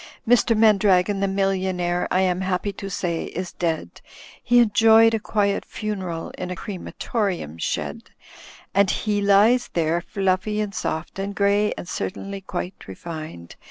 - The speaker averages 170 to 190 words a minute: No, average, 145 wpm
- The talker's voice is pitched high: Yes, high, 195 Hz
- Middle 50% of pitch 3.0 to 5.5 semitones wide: No, narrow, 2.6 semitones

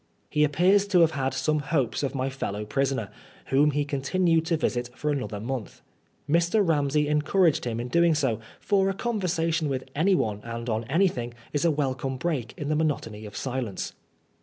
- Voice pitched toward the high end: No, medium, 145 Hz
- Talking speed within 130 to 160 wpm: No, average, 185 wpm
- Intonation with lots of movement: No, average, 4.6 semitones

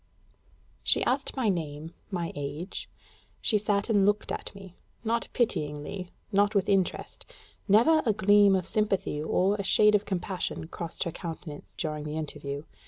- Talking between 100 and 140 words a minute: No, average, 155 wpm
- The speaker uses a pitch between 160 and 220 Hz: Yes, high, 190 Hz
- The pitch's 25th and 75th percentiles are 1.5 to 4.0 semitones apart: No, average, 4.5 semitones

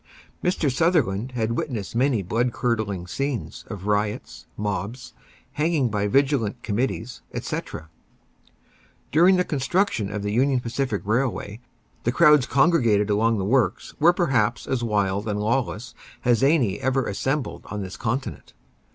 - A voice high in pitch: No, low, 120 Hz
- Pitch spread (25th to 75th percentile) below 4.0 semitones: No, average, 4.7 semitones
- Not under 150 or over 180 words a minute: No, slow, 135 wpm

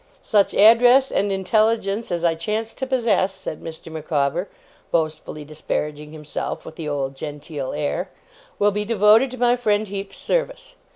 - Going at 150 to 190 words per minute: Yes, average, 155 wpm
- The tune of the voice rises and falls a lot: Yes, wide, 6.3 semitones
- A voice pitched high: Yes, high, 195 Hz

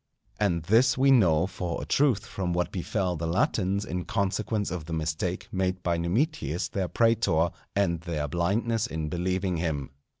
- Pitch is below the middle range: Yes, very low, 90 Hz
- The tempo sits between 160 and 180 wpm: Yes, average, 165 wpm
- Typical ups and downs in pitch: Yes, average, 3.6 semitones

